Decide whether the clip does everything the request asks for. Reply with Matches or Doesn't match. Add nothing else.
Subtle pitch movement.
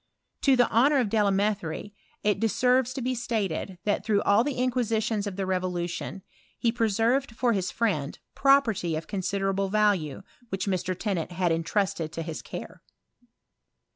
Doesn't match